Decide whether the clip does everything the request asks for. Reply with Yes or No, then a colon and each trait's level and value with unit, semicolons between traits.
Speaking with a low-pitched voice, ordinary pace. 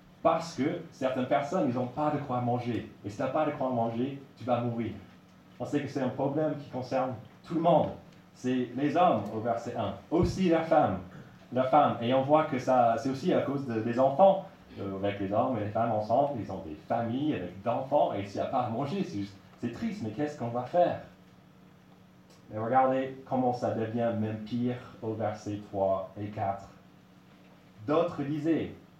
Yes: low, 125 Hz; average, 205 wpm